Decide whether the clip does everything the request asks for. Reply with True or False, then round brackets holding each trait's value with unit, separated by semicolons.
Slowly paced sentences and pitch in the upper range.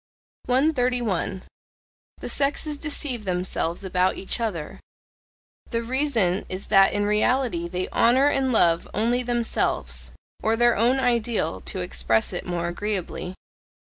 True (125 wpm; 215 Hz)